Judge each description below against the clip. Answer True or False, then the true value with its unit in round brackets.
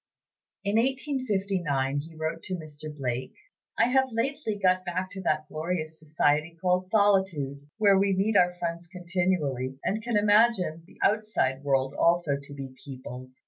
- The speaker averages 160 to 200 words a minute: False (150 wpm)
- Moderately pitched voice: True (175 Hz)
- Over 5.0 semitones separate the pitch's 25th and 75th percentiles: True (5.5 semitones)